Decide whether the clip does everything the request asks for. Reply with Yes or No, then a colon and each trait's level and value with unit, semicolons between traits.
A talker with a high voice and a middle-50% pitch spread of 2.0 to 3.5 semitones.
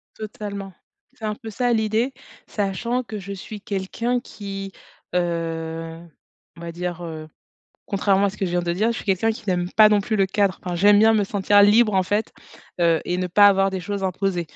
Yes: high, 195 Hz; average, 3.0 semitones